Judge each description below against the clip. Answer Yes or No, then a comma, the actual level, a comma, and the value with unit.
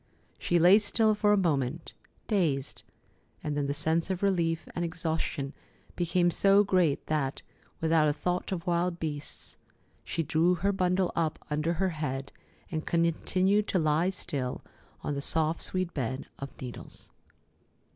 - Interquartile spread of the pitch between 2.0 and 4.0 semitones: Yes, average, 3.4 semitones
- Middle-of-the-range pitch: Yes, medium, 165 Hz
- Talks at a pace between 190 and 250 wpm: No, average, 150 wpm